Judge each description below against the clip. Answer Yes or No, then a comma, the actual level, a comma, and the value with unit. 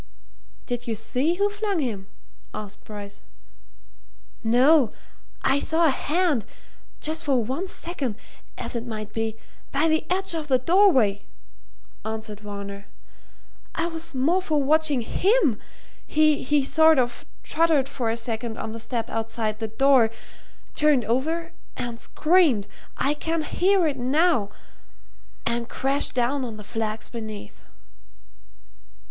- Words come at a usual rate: No, slow, 130 wpm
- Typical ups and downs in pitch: No, wide, 6.0 semitones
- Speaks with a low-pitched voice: No, very high, 260 Hz